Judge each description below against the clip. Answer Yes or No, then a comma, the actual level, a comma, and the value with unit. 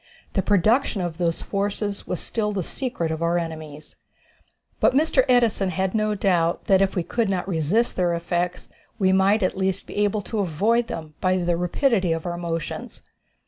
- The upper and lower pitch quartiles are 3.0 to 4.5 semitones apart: Yes, average, 3.4 semitones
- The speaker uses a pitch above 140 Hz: Yes, high, 190 Hz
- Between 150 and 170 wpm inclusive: No, average, 185 wpm